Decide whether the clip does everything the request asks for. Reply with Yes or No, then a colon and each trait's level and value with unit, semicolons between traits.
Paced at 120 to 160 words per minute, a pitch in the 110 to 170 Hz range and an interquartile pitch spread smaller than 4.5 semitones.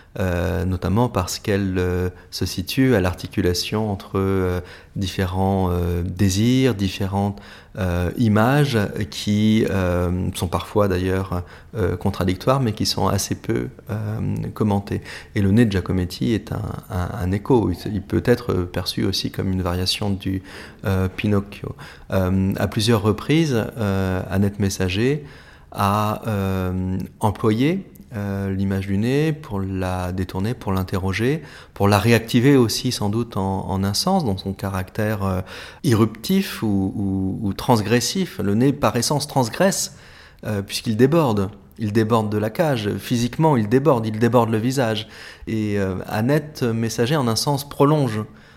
No: slow, 145 wpm; low, 100 Hz; average, 3.8 semitones